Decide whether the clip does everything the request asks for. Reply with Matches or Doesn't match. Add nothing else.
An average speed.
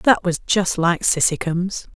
Matches